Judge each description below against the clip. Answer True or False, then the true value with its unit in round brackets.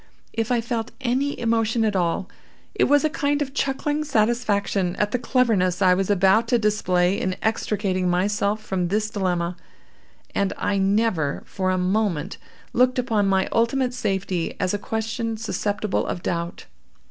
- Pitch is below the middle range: False (210 Hz)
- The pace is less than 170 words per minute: True (160 wpm)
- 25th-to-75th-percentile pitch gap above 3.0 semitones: True (3.8 semitones)